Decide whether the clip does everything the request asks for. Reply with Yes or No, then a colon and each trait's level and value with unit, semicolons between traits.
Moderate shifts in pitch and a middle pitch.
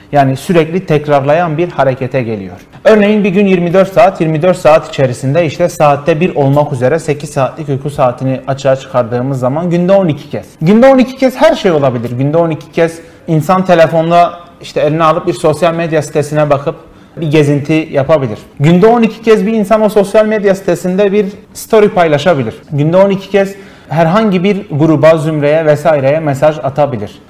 Yes: average, 4.7 semitones; medium, 160 Hz